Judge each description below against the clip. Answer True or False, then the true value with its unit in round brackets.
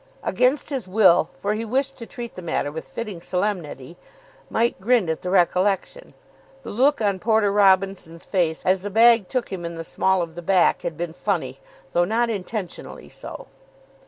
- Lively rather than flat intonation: False (4.5 semitones)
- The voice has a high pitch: True (195 Hz)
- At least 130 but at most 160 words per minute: False (180 wpm)